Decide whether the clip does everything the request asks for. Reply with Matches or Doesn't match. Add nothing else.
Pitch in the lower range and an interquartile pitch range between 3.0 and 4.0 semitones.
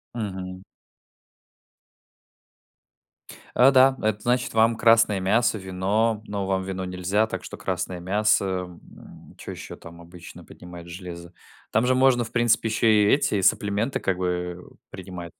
Matches